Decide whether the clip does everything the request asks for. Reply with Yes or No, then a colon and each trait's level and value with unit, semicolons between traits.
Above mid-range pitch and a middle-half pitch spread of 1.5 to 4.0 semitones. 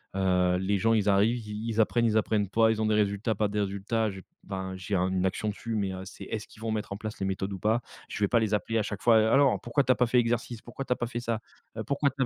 No: low, 105 Hz; average, 2.7 semitones